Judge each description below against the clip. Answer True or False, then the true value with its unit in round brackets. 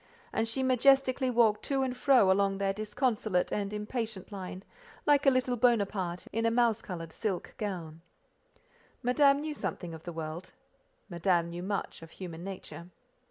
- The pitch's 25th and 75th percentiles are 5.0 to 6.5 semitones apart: True (5.6 semitones)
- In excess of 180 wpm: False (160 wpm)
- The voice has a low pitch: False (210 Hz)